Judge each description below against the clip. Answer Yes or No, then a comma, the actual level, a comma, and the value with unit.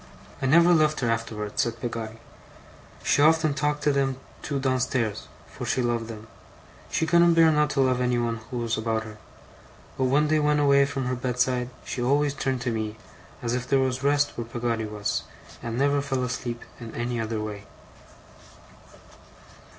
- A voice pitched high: No, low, 125 Hz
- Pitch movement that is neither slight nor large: Yes, average, 3.6 semitones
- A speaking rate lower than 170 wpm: No, average, 180 wpm